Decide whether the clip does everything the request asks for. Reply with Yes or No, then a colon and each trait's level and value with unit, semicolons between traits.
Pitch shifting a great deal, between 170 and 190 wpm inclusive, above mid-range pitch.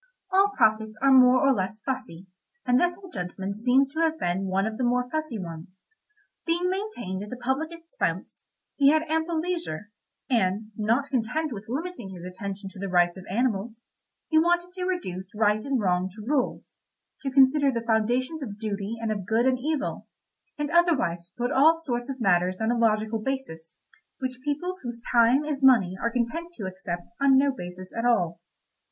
Yes: wide, 6.3 semitones; average, 185 wpm; high, 240 Hz